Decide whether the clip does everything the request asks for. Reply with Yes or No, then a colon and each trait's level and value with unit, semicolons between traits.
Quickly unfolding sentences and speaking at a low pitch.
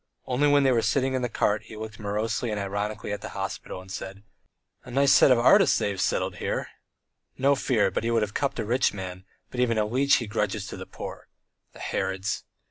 Yes: fast, 225 wpm; low, 110 Hz